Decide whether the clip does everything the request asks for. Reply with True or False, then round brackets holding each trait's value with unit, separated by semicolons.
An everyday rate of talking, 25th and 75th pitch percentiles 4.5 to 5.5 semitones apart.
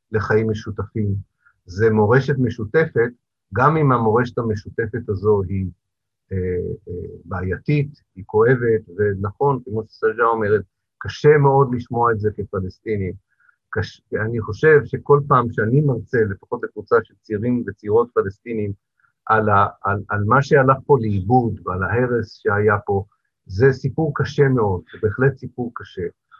True (135 wpm; 4.8 semitones)